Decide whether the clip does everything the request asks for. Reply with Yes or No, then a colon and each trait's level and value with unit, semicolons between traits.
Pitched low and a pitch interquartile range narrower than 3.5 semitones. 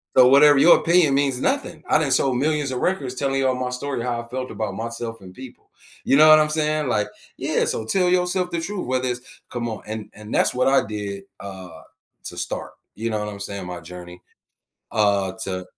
No: low, 125 Hz; average, 5.3 semitones